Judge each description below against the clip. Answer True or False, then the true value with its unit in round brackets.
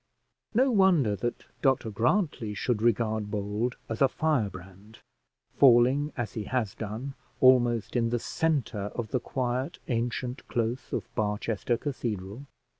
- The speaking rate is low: True (130 wpm)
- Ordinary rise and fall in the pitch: True (3.4 semitones)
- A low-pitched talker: True (120 Hz)